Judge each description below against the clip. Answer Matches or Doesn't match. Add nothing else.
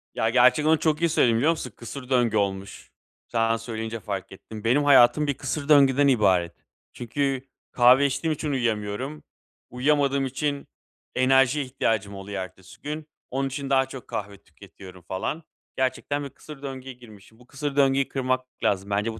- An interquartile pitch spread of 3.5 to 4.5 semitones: Matches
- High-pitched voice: Doesn't match